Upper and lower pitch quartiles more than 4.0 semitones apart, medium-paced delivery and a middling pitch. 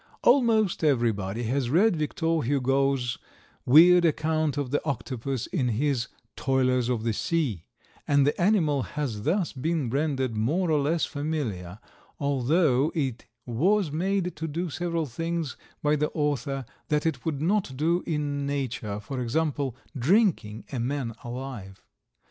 Yes: average, 4.4 semitones; average, 145 wpm; medium, 145 Hz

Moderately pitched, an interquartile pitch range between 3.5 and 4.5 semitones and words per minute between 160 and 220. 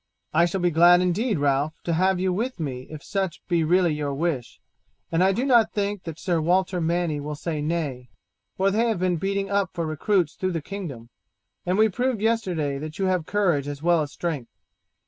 Yes: medium, 175 Hz; average, 4.0 semitones; fast, 205 wpm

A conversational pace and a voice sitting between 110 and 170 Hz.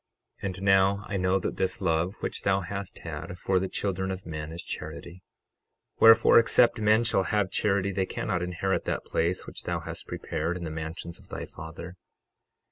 No: average, 190 wpm; very low, 95 Hz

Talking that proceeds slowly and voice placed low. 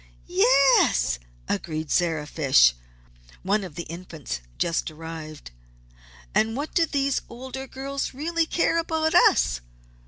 No: slow, 120 wpm; high, 190 Hz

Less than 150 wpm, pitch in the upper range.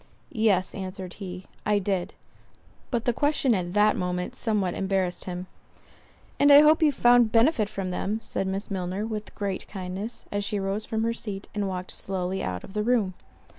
No: average, 180 wpm; high, 200 Hz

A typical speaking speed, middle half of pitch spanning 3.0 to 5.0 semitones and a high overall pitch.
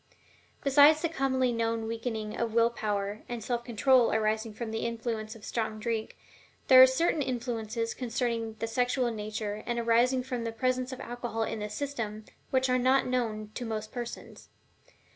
No: average, 170 wpm; narrow, 2.4 semitones; high, 235 Hz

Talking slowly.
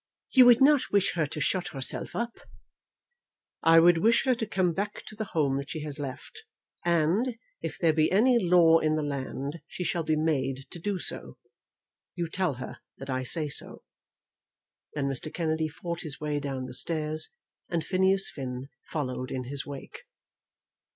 No: average, 180 wpm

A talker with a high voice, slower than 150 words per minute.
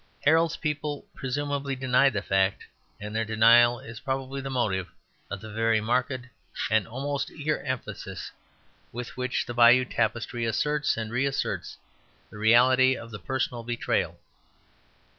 No: low, 125 Hz; average, 140 wpm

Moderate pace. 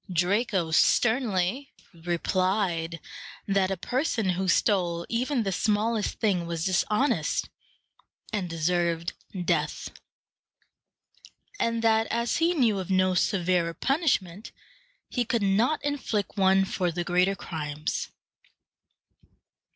No: slow, 105 wpm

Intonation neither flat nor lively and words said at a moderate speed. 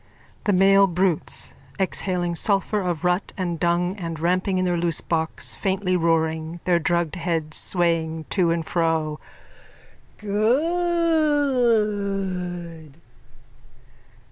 No: average, 3.0 semitones; slow, 105 wpm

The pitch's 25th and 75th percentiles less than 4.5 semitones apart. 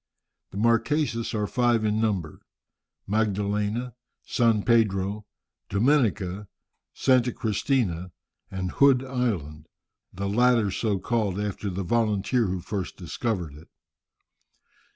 Yes: average, 3.5 semitones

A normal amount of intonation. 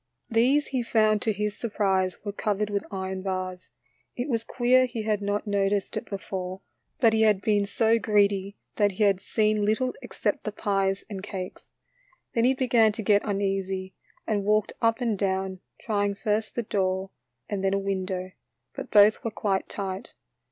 No: narrow, 2.2 semitones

